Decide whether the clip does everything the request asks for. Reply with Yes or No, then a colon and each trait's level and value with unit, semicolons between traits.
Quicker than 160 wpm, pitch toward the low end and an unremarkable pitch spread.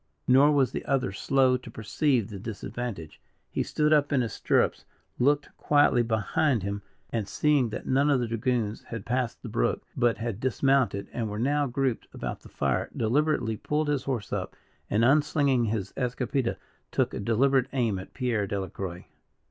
Yes: average, 170 wpm; low, 125 Hz; average, 4.0 semitones